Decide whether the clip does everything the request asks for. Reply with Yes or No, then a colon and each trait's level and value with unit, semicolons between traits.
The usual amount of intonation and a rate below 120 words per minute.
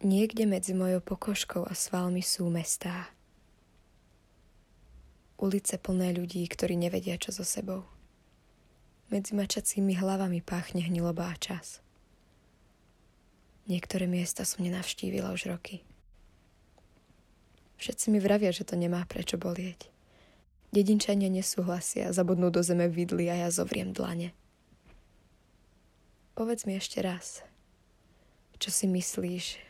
No: narrow, 2.2 semitones; slow, 110 wpm